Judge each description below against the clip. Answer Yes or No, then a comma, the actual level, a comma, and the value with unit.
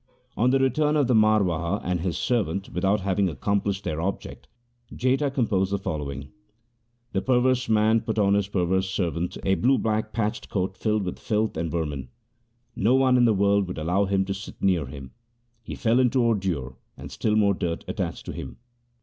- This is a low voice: Yes, low, 100 Hz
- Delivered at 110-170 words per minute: No, average, 195 wpm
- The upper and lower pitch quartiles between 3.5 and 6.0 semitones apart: Yes, average, 4.1 semitones